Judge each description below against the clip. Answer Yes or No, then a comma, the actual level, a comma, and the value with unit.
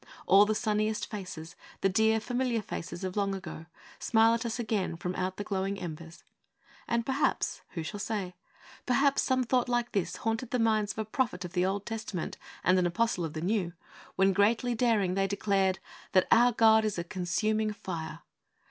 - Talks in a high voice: Yes, high, 205 Hz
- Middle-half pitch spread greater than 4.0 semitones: No, average, 3.5 semitones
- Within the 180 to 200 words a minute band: Yes, average, 190 wpm